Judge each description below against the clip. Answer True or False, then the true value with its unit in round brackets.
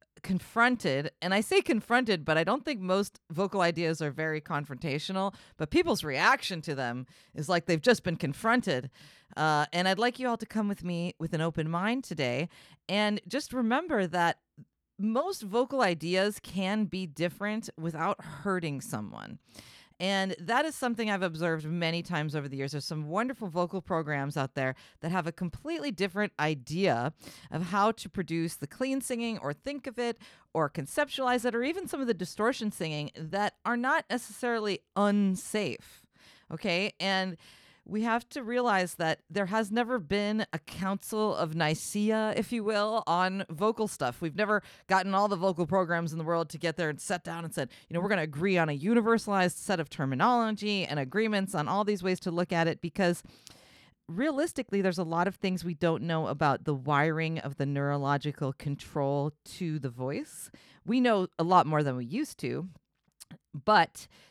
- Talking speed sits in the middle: True (180 wpm)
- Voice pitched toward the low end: False (185 Hz)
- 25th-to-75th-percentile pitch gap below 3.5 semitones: False (5.1 semitones)